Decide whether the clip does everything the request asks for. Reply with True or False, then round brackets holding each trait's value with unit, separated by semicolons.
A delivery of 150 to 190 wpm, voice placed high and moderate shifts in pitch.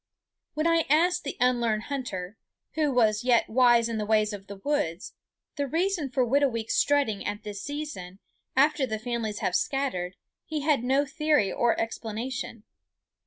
True (160 wpm; 245 Hz; 5.0 semitones)